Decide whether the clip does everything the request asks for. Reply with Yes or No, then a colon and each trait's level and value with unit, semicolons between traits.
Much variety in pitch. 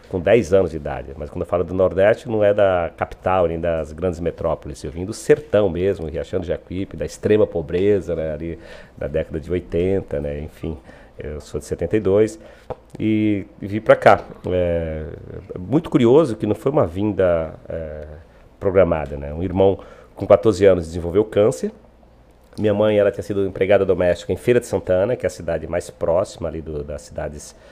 No: average, 4.1 semitones